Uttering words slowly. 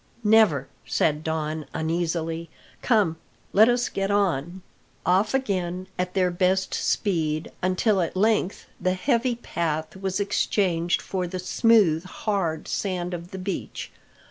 Yes: slow, 130 wpm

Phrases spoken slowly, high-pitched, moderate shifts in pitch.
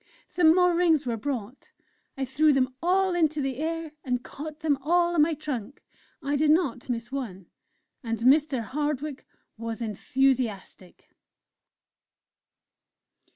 Yes: slow, 130 wpm; very high, 280 Hz; average, 4.1 semitones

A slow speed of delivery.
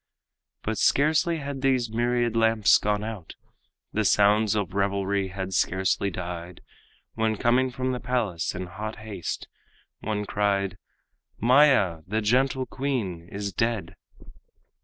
Yes: slow, 125 wpm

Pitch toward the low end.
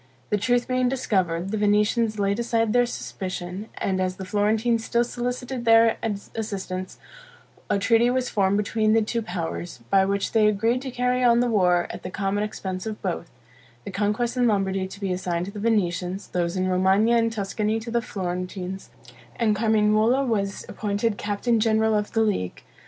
No: high, 210 Hz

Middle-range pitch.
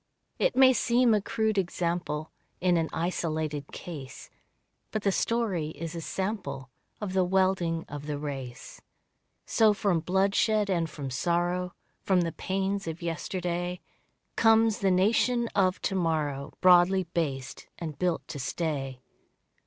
Yes: medium, 175 Hz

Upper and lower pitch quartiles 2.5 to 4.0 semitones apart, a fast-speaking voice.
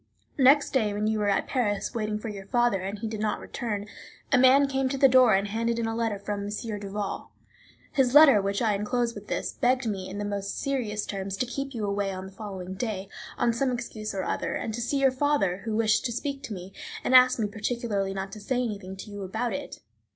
Yes: average, 3.6 semitones; fast, 240 wpm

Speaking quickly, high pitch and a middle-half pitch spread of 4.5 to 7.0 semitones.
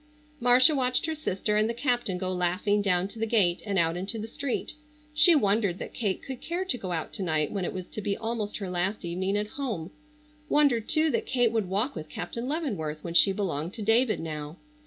Yes: fast, 220 wpm; high, 210 Hz; average, 5.2 semitones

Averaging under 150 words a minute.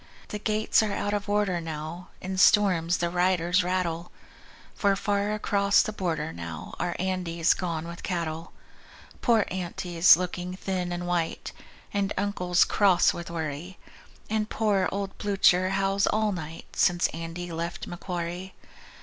Yes: average, 140 wpm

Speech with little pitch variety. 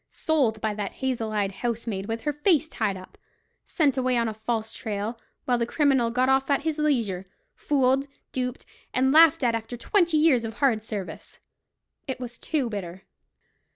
No: average, 4.0 semitones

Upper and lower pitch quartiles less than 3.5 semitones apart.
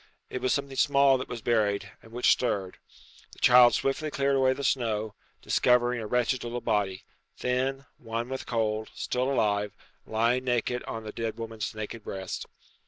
Yes: average, 2.8 semitones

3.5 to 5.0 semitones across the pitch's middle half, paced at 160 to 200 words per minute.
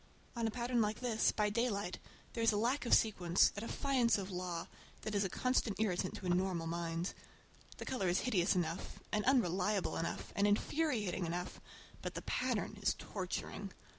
Yes: average, 4.5 semitones; average, 180 wpm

